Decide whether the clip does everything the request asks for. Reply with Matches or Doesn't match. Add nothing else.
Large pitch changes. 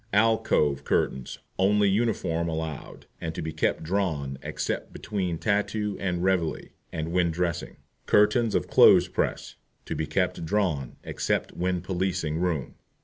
Doesn't match